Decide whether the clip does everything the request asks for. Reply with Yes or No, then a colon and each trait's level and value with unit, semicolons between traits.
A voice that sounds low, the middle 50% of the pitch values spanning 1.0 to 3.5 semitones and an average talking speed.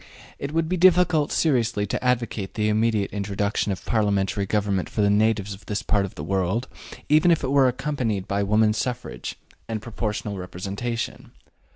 No: low, 110 Hz; average, 3.9 semitones; average, 170 wpm